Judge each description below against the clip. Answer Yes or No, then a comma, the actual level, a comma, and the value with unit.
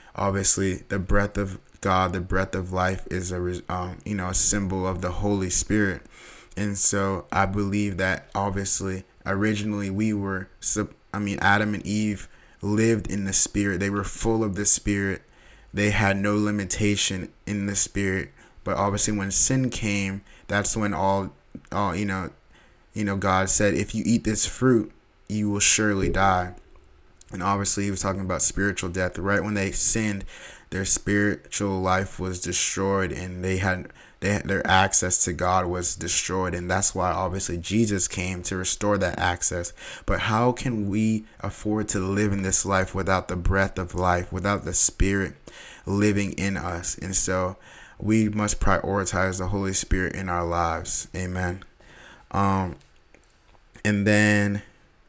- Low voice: Yes, very low, 95 Hz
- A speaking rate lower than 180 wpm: Yes, average, 160 wpm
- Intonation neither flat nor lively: No, narrow, 1.8 semitones